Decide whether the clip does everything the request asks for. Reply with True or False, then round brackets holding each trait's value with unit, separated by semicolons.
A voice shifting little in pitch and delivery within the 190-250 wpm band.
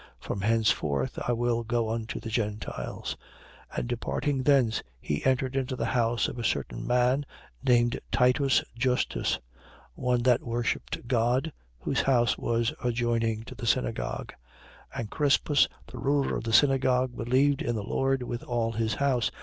False (2.2 semitones; 160 wpm)